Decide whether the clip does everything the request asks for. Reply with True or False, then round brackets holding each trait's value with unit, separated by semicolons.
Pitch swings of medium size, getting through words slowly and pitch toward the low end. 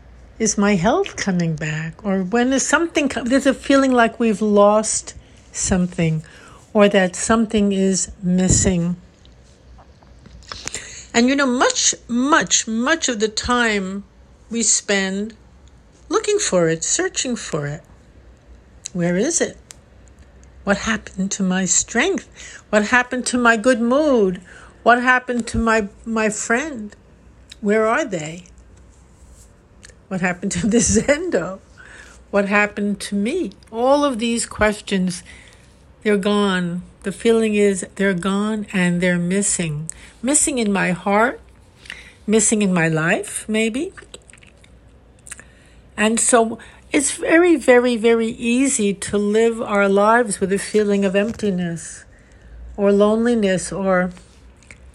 False (4.1 semitones; 125 wpm; 210 Hz)